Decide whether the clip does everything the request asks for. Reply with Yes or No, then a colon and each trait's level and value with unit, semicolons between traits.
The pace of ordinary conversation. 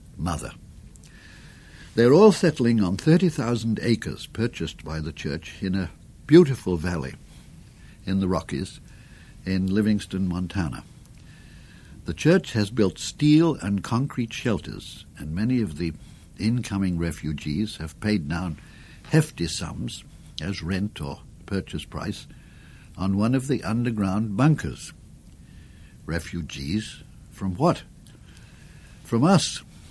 No: slow, 110 wpm